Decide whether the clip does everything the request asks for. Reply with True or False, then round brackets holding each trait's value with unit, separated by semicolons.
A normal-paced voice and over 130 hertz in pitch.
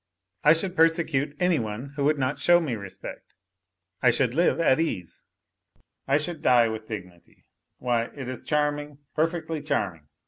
True (160 wpm; 140 Hz)